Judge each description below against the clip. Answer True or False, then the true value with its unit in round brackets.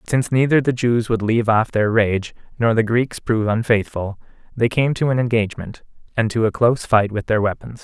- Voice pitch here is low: True (115 Hz)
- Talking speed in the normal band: False (215 wpm)